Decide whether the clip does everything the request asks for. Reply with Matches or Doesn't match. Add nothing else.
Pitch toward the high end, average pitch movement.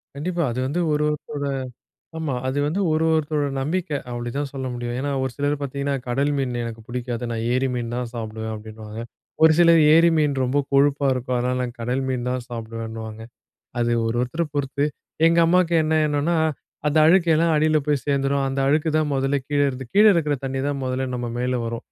Doesn't match